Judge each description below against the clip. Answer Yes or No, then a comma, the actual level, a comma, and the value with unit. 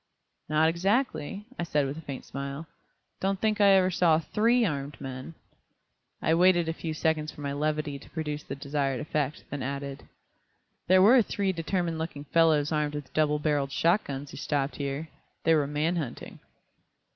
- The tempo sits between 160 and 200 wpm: Yes, average, 175 wpm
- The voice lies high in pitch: No, medium, 155 Hz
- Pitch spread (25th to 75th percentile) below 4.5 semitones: Yes, average, 3.2 semitones